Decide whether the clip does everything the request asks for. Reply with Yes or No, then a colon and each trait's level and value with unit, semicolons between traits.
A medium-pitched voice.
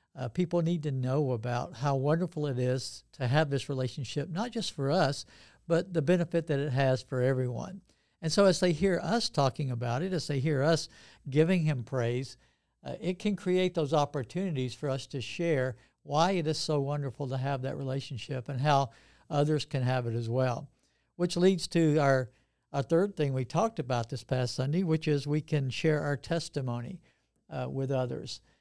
Yes: medium, 145 Hz